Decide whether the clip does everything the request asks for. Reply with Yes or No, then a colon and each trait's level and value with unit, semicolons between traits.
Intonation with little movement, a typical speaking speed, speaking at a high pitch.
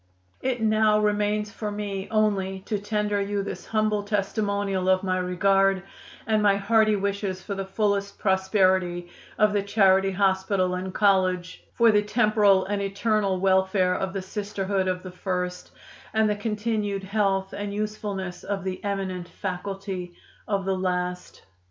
Yes: narrow, 1.8 semitones; average, 150 wpm; high, 195 Hz